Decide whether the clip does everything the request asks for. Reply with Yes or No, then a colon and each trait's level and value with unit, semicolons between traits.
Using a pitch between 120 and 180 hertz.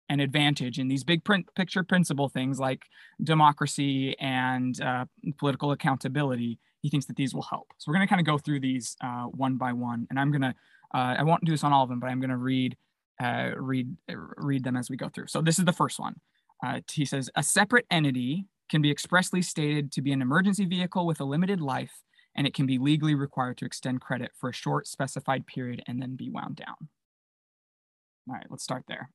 Yes: medium, 140 Hz